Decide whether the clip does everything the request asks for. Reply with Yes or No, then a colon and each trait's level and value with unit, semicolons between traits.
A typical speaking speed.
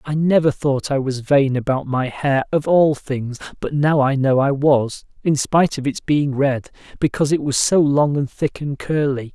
No: fast, 210 wpm